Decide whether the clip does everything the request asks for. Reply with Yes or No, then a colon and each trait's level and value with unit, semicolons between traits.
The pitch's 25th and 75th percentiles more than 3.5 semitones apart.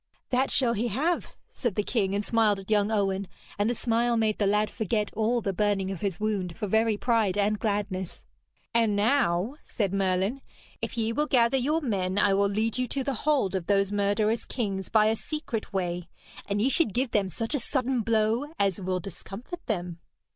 No: average, 3.1 semitones